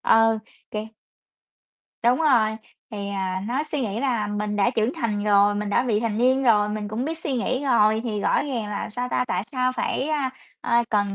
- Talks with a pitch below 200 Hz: No, high, 225 Hz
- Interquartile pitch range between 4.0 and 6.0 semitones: No, average, 3.4 semitones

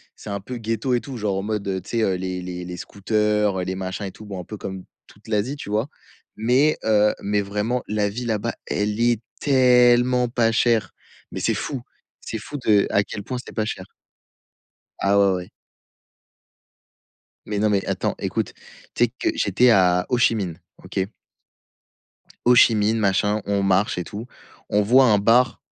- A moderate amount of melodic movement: Yes, average, 3.2 semitones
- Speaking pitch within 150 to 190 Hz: No, low, 105 Hz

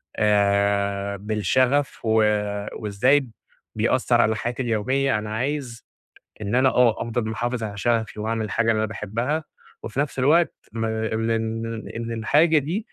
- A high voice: No, low, 115 Hz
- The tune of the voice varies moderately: Yes, average, 3.3 semitones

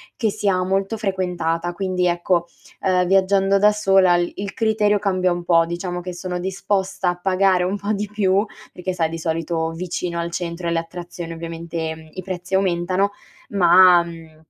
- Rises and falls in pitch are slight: Yes, narrow, 2.1 semitones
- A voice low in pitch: No, medium, 180 Hz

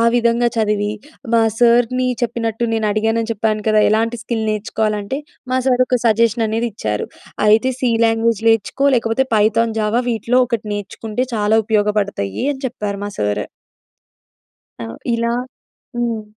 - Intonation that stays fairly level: Yes, narrow, 1.8 semitones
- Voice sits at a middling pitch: No, high, 225 Hz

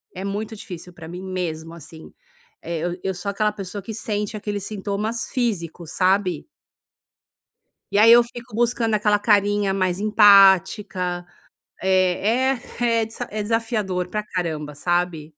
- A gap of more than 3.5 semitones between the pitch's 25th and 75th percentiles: No, average, 3.1 semitones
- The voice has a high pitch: Yes, high, 200 Hz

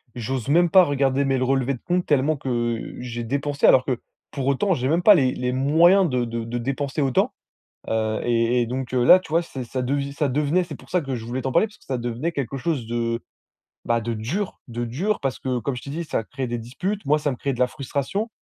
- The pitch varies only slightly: No, average, 3.6 semitones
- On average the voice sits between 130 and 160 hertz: Yes, low, 135 Hz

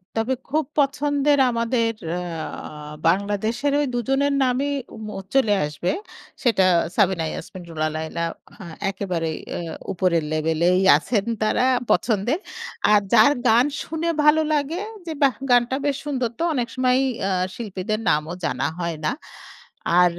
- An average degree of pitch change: No, wide, 7.2 semitones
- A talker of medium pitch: No, high, 225 Hz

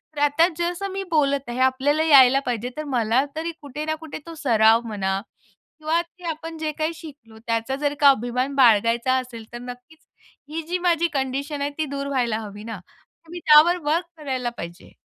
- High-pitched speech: Yes, very high, 280 Hz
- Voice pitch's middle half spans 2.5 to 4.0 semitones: No, average, 4.7 semitones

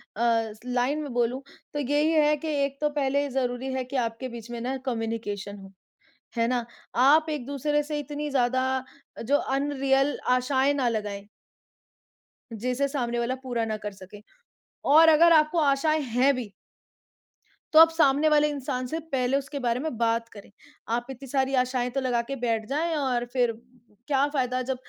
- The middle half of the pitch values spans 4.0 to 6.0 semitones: No, average, 3.3 semitones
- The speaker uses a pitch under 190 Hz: No, very high, 260 Hz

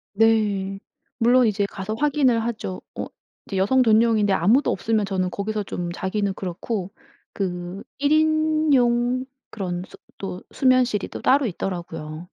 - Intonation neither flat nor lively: Yes, average, 4.6 semitones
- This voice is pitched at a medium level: No, high, 215 Hz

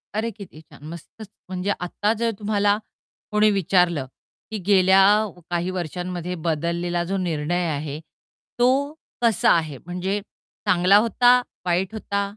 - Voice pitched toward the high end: No, medium, 180 Hz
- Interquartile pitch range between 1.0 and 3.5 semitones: Yes, average, 3.0 semitones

